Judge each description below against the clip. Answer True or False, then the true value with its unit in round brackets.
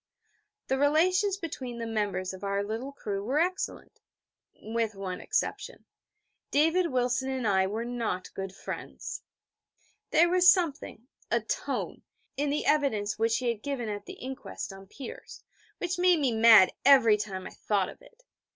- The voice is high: True (245 Hz)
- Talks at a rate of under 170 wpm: True (160 wpm)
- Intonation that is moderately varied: False (6.7 semitones)